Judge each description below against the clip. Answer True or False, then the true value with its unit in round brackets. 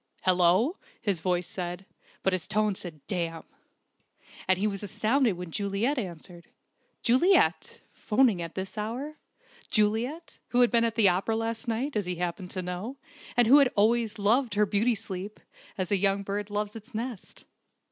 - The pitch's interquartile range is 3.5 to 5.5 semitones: True (3.9 semitones)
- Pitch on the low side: False (210 Hz)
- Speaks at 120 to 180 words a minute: True (165 wpm)